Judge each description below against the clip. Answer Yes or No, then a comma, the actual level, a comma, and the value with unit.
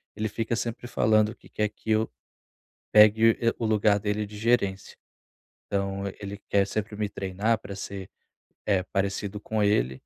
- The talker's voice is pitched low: Yes, low, 105 Hz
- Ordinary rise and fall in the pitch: No, narrow, 1.7 semitones